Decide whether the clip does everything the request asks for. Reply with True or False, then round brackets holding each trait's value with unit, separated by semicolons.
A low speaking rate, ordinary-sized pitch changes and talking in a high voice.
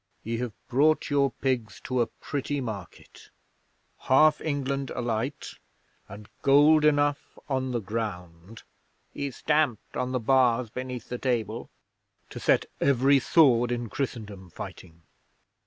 False (125 wpm; 3.6 semitones; 125 Hz)